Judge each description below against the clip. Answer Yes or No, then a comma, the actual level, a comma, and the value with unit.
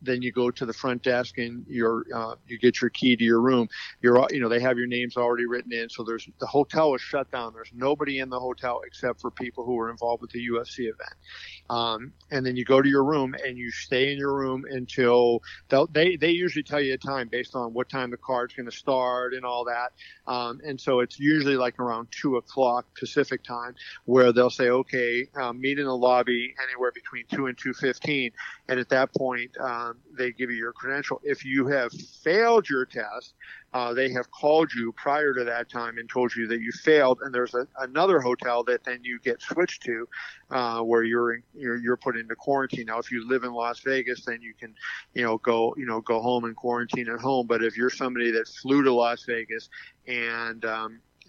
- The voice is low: Yes, low, 125 Hz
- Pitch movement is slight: Yes, narrow, 1.7 semitones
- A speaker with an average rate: No, fast, 225 wpm